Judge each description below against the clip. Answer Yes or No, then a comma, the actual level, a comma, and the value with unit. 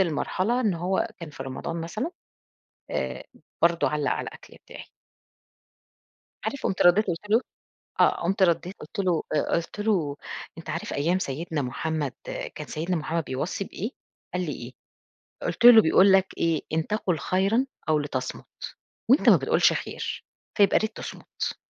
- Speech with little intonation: No, average, 4.2 semitones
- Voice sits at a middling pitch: Yes, medium, 170 Hz